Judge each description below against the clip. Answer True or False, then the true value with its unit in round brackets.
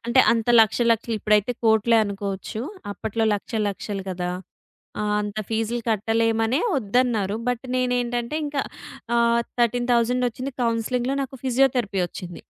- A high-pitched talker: True (230 Hz)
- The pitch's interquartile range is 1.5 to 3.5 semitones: True (2.6 semitones)